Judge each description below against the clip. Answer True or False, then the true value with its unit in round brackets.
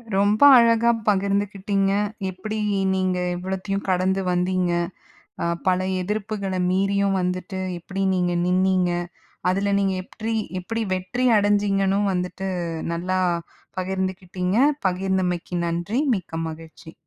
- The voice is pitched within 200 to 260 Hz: False (190 Hz)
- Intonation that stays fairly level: True (1.6 semitones)